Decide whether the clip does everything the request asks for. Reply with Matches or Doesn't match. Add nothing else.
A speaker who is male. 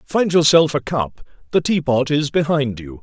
Matches